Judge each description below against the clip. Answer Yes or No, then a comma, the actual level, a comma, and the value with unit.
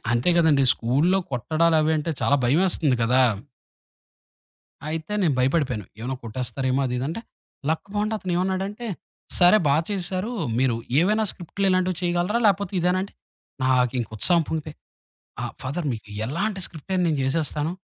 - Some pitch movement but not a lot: No, wide, 6.0 semitones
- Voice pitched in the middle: Yes, medium, 160 Hz